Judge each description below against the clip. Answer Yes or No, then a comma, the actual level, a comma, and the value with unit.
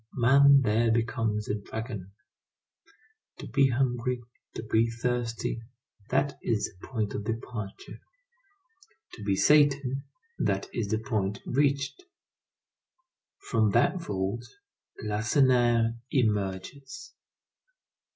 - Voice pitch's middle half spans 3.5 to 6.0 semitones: Yes, average, 3.8 semitones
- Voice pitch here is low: Yes, low, 115 Hz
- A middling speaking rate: No, slow, 95 wpm